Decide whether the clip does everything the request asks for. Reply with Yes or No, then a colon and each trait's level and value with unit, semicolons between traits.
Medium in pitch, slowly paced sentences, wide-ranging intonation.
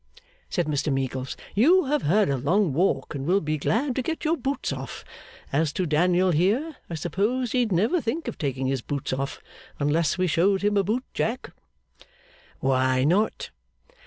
No: medium, 180 Hz; average, 175 wpm; wide, 8.0 semitones